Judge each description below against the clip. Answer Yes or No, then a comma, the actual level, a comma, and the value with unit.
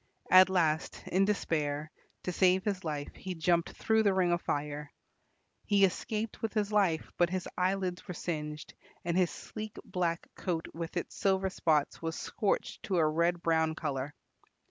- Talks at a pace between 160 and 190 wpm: Yes, average, 165 wpm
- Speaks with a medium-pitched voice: Yes, medium, 175 Hz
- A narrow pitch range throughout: No, average, 3.1 semitones